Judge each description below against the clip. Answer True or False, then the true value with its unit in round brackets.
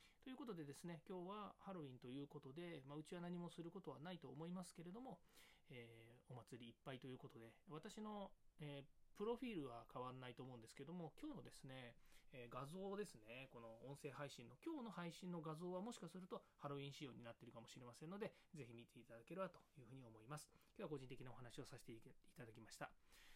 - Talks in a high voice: False (145 Hz)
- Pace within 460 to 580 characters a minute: True (470 characters per minute)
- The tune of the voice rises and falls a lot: True (6.0 semitones)